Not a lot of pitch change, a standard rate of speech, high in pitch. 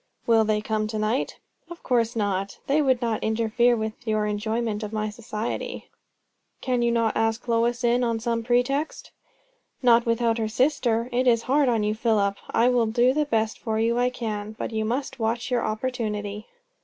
Yes: narrow, 2.0 semitones; average, 180 wpm; high, 230 Hz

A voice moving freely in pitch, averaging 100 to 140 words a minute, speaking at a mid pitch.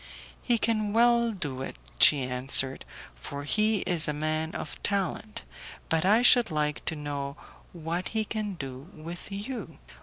No: wide, 6.6 semitones; average, 155 wpm; medium, 170 Hz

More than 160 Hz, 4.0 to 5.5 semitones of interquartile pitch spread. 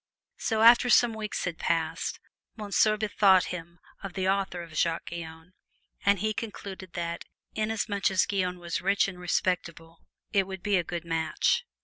No: high, 190 Hz; average, 3.2 semitones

